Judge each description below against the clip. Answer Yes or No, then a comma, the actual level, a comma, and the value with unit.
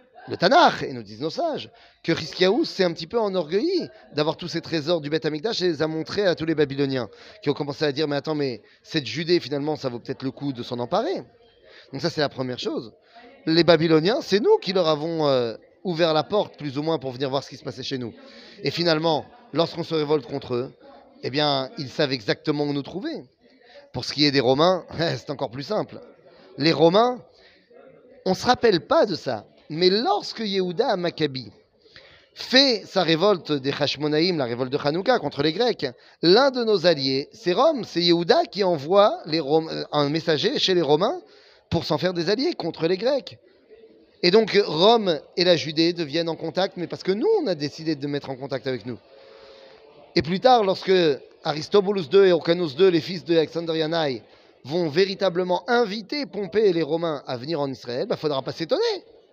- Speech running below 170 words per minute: No, average, 205 wpm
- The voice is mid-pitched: Yes, medium, 165 Hz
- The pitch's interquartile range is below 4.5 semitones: No, average, 5.1 semitones